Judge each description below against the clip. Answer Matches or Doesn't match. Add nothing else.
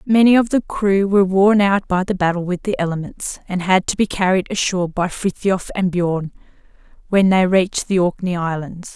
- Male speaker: Doesn't match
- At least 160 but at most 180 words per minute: Doesn't match